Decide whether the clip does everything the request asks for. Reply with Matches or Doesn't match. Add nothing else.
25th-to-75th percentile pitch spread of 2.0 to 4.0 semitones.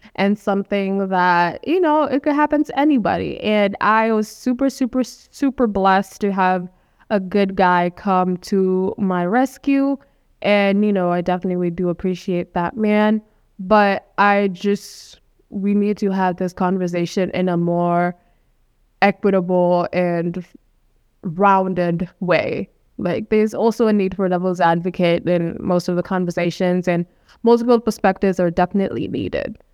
Matches